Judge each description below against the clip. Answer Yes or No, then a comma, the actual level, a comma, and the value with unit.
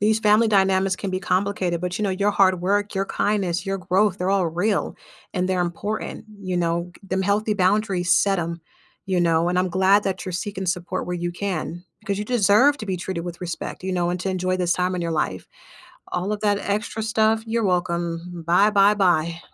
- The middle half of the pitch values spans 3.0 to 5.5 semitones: No, narrow, 2.4 semitones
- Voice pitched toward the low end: No, medium, 185 Hz